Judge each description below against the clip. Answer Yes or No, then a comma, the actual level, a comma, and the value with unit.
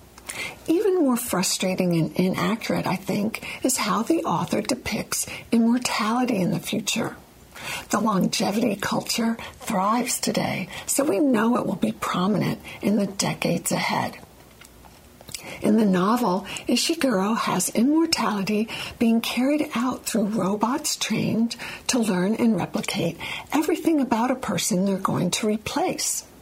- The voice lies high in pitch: Yes, high, 220 Hz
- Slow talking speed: Yes, slow, 125 wpm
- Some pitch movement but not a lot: Yes, average, 4.7 semitones